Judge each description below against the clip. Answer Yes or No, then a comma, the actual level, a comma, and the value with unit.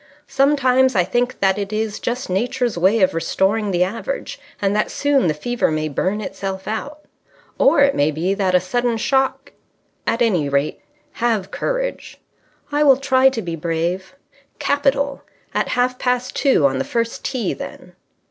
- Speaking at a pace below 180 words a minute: Yes, average, 165 wpm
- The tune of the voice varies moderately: No, wide, 5.9 semitones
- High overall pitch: Yes, high, 225 Hz